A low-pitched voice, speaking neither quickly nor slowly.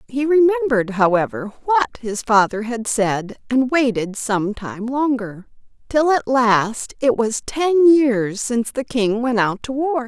No: high, 240 Hz; average, 160 wpm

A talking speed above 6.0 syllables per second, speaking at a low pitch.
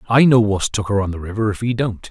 Yes: 6.2 syllables/s; low, 110 Hz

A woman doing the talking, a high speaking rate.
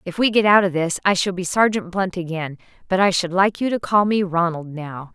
Yes: female; fast, 255 wpm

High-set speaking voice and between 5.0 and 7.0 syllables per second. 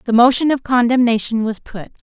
Yes: high, 240 Hz; 5.7 syllables/s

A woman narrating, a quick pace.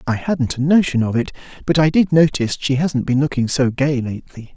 No: male; fast, 225 wpm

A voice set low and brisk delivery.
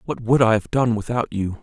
Yes: low, 115 Hz; fast, 260 wpm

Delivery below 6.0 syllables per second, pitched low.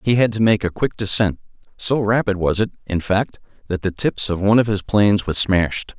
Yes: 5.5 syllables/s; low, 100 Hz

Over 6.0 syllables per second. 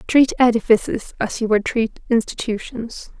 No: 4.6 syllables/s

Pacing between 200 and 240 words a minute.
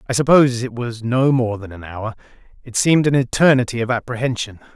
No: average, 190 wpm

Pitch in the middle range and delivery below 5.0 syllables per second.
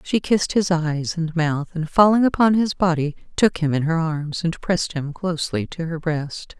Yes: medium, 165 Hz; 4.8 syllables/s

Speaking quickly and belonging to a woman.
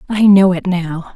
Yes: fast, 210 wpm; female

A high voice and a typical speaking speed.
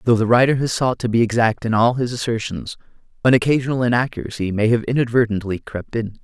No: low, 115 Hz; average, 190 wpm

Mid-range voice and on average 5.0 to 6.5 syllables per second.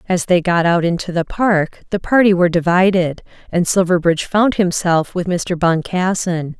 No: medium, 180 Hz; 4.8 syllables/s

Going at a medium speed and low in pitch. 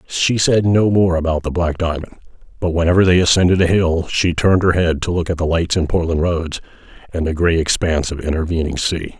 No: fast, 215 wpm; very low, 85 Hz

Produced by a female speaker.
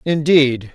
No: male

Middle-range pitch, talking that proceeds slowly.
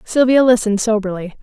No: high, 225 Hz; slow, 125 wpm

